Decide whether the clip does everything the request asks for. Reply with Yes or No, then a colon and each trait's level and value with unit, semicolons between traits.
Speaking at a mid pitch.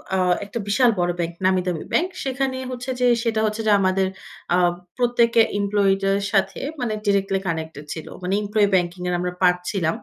No: high, 195 Hz